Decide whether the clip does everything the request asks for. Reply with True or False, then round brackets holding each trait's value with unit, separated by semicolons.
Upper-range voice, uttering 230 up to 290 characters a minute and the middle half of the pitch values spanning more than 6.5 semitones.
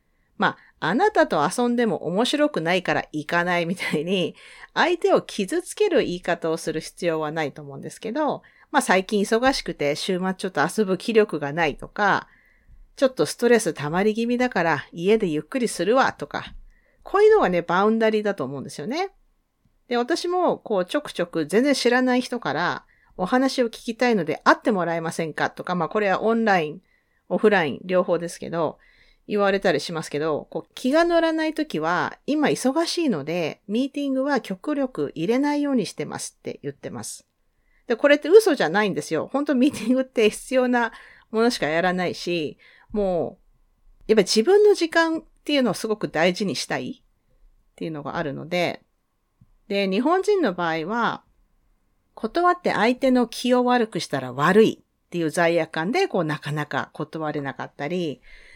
False (215 Hz; 360 characters per minute; 7.6 semitones)